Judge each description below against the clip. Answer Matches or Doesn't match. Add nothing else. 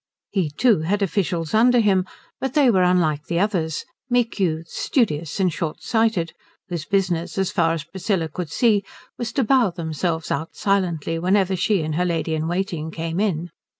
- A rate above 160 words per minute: Matches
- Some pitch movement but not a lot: Matches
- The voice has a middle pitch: Matches